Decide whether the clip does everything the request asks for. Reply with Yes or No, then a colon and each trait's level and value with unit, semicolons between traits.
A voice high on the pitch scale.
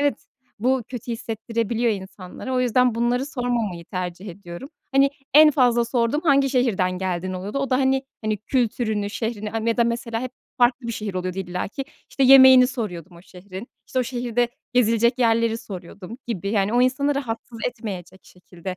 Yes: high, 230 Hz